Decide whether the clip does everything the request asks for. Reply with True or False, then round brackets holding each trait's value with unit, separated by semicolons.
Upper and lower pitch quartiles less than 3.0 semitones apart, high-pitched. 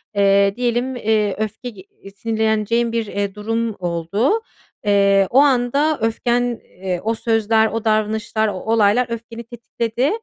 True (2.6 semitones; 220 Hz)